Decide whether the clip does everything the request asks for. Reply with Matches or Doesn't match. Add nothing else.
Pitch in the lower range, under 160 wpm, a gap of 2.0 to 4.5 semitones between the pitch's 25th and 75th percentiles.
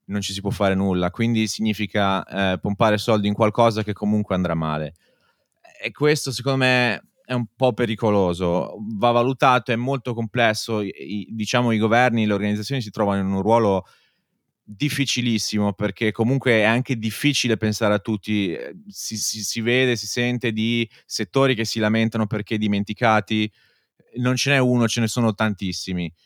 Doesn't match